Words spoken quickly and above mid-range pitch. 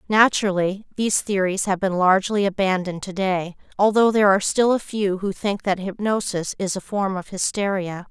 No: average, 170 wpm; high, 195 Hz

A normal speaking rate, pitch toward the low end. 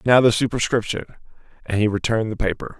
Yes: average, 170 wpm; low, 110 Hz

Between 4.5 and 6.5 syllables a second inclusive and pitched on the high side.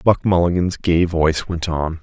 No: 4.7 syllables/s; very low, 85 Hz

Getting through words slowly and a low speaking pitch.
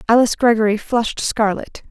No: slow, 125 wpm; high, 225 Hz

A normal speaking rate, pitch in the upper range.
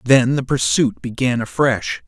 No: average, 145 wpm; low, 120 Hz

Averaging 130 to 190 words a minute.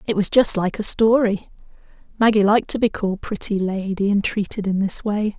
No: average, 200 wpm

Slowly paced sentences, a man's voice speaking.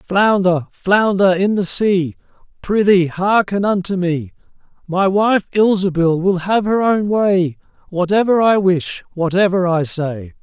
Yes: slow, 130 wpm; male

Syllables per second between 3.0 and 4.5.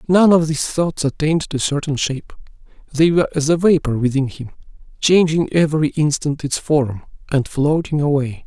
No: 5.4 syllables/s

